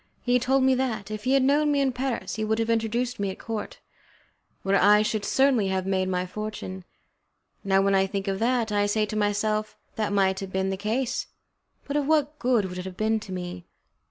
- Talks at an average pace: No, fast, 225 wpm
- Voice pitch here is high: Yes, high, 215 Hz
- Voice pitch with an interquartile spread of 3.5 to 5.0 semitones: Yes, average, 4.3 semitones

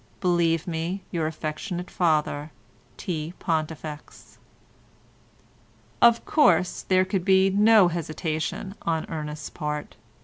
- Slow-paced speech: Yes, slow, 100 wpm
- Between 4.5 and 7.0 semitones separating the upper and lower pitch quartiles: No, average, 3.1 semitones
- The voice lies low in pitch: No, medium, 165 Hz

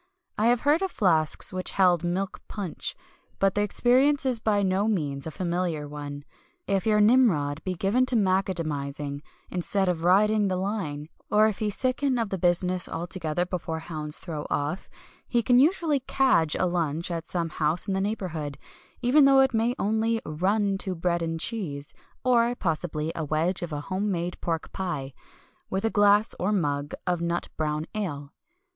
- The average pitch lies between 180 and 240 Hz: Yes, medium, 185 Hz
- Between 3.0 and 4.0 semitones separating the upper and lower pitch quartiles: No, average, 5.0 semitones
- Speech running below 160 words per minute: No, average, 175 wpm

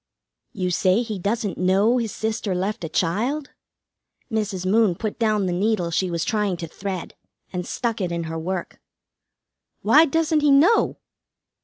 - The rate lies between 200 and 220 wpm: No, average, 160 wpm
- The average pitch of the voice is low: No, high, 205 Hz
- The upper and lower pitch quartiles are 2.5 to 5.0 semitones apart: Yes, average, 4.0 semitones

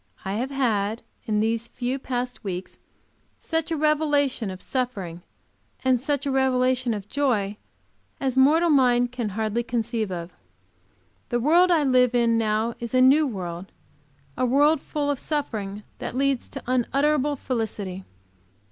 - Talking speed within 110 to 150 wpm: Yes, average, 145 wpm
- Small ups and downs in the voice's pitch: No, average, 4.1 semitones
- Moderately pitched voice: No, very high, 250 Hz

